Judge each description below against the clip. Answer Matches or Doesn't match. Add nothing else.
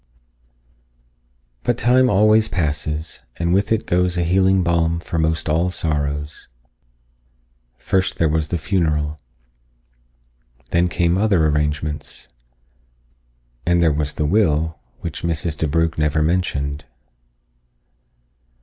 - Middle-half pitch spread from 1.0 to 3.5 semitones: Matches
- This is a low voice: Matches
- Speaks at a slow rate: Matches